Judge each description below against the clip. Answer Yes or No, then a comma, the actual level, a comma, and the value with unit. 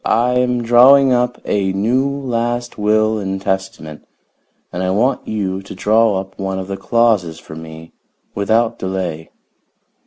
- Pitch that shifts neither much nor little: Yes, average, 4.0 semitones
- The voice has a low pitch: Yes, low, 105 Hz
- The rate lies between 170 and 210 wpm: No, average, 150 wpm